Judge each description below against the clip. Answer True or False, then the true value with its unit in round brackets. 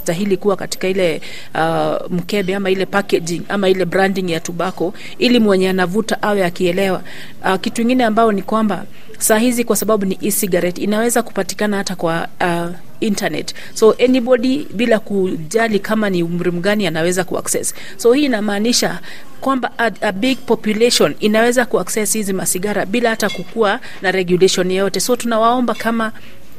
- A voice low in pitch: False (200 Hz)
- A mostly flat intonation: False (3.5 semitones)